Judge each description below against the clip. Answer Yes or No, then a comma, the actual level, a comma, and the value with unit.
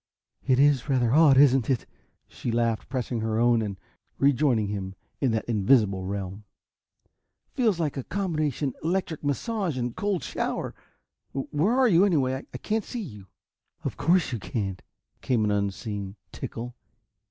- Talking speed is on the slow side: No, average, 150 wpm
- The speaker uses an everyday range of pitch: No, wide, 6.1 semitones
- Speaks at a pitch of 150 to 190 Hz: No, low, 130 Hz